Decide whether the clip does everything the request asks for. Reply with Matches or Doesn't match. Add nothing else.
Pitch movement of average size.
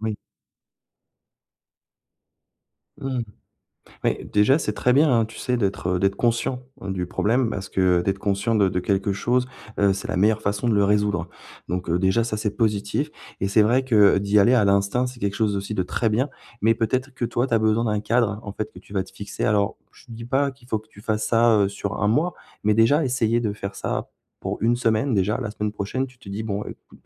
Matches